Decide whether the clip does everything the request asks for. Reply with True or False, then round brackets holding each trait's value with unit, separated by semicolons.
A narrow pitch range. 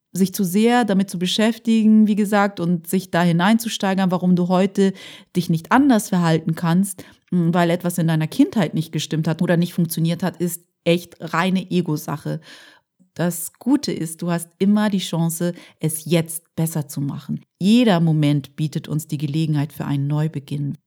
False (3.0 semitones)